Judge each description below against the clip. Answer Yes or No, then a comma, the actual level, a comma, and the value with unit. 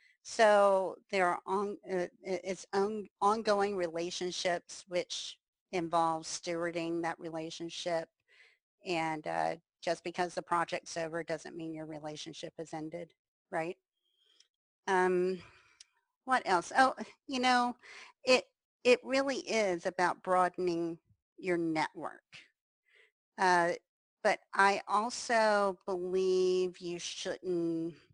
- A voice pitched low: No, medium, 180 Hz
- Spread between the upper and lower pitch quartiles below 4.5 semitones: Yes, average, 3.2 semitones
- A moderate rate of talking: No, slow, 105 wpm